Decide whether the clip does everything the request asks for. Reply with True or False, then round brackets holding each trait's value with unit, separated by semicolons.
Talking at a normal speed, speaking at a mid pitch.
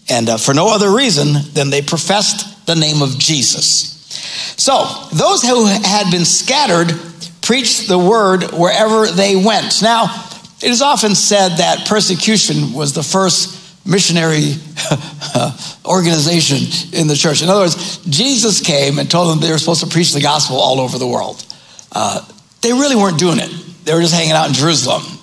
True (170 wpm; 170 Hz)